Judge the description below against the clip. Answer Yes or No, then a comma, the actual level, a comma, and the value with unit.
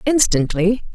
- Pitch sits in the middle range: No, high, 215 Hz